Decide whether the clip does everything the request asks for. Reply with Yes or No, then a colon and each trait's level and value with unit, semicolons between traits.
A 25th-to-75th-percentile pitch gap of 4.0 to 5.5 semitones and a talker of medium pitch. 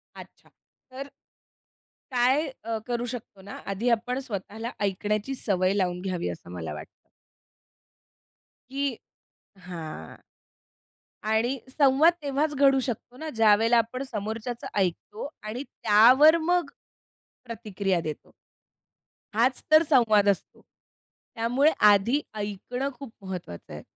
No: average, 4.9 semitones; high, 225 Hz